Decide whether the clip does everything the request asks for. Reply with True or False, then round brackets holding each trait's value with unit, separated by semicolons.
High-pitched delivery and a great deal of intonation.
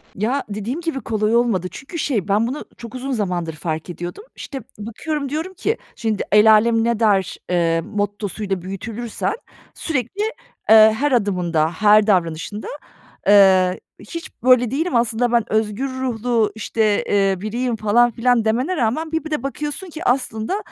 False (225 Hz; 4.1 semitones)